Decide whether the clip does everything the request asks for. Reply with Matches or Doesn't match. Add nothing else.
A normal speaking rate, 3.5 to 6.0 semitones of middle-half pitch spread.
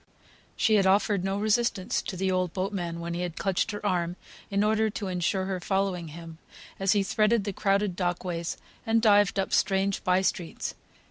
Doesn't match